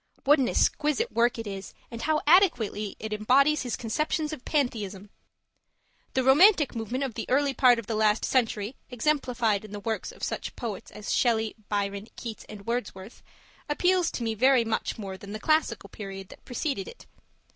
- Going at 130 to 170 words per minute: No, average, 180 wpm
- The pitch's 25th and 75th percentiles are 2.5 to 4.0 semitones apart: No, average, 4.8 semitones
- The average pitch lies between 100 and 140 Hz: No, high, 235 Hz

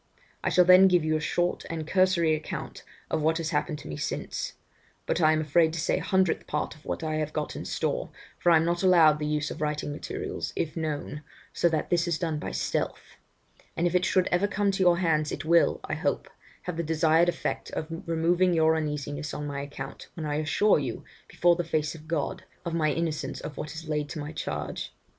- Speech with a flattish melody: Yes, narrow, 2.3 semitones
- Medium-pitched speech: Yes, medium, 160 Hz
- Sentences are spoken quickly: Yes, fast, 225 wpm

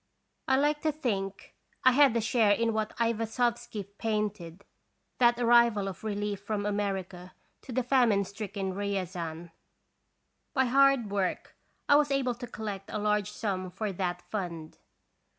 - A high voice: Yes, high, 210 Hz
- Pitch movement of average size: Yes, average, 3.6 semitones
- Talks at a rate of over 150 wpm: No, average, 145 wpm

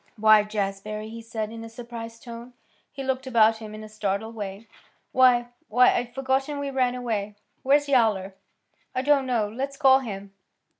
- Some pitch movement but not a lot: Yes, average, 3.3 semitones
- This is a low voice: No, high, 230 Hz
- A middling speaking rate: Yes, average, 170 wpm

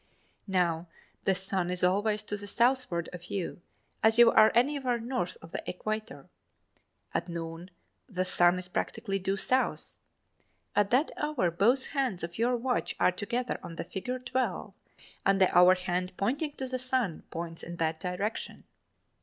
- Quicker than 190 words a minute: No, average, 160 wpm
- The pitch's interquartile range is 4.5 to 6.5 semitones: Yes, wide, 5.4 semitones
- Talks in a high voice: Yes, high, 195 Hz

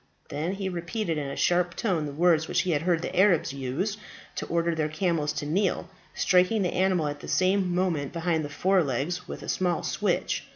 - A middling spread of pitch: Yes, average, 3.3 semitones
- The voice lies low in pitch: No, medium, 175 Hz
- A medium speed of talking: No, fast, 210 wpm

